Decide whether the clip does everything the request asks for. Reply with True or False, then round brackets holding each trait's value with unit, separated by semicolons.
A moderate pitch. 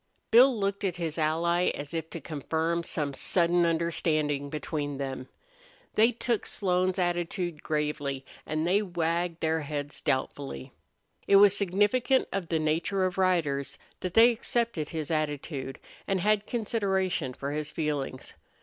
True (170 Hz)